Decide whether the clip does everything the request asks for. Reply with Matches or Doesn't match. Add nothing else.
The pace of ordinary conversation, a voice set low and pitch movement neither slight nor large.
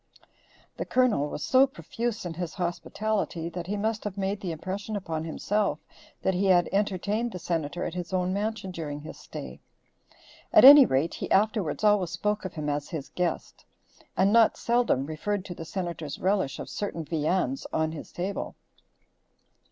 Doesn't match